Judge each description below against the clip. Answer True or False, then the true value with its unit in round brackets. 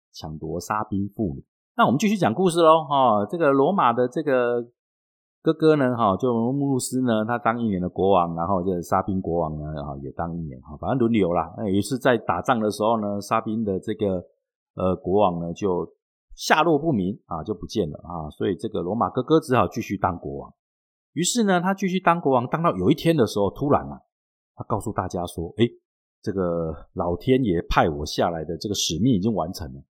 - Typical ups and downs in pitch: False (6.8 semitones)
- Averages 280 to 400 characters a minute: True (300 characters per minute)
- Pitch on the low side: True (105 Hz)